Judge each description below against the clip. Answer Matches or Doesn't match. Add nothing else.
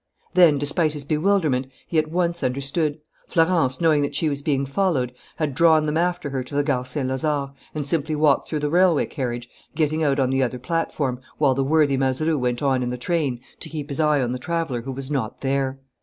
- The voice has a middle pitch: Matches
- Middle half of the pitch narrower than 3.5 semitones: Matches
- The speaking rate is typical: Doesn't match